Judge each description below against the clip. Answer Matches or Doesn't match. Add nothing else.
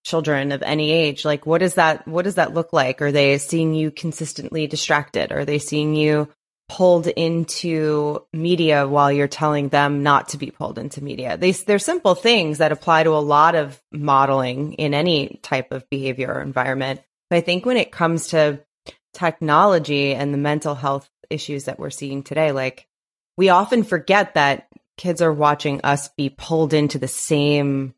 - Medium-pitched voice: Matches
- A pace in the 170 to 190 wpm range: Matches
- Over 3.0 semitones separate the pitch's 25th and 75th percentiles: Doesn't match